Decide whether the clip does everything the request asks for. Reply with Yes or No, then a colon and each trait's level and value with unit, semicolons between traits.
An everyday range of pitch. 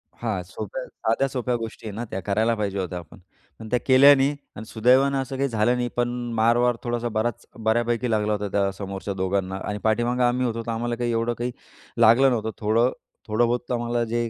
No: narrow, 2.3 semitones